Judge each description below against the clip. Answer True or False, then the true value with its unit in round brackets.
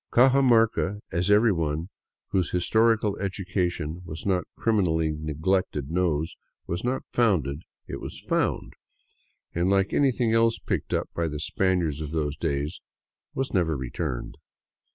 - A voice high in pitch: False (90 Hz)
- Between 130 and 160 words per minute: True (140 wpm)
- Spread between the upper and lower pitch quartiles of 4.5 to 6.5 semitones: True (5.2 semitones)